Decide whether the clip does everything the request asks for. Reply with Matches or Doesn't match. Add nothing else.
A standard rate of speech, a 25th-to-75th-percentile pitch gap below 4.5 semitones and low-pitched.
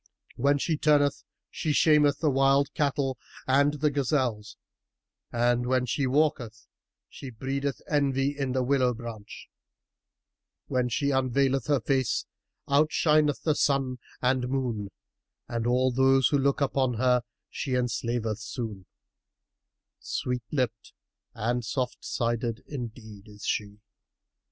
Doesn't match